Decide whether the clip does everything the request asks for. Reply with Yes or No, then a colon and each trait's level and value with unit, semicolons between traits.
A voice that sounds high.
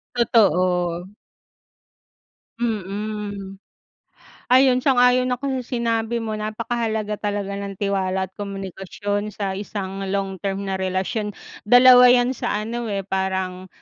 Yes: high, 205 Hz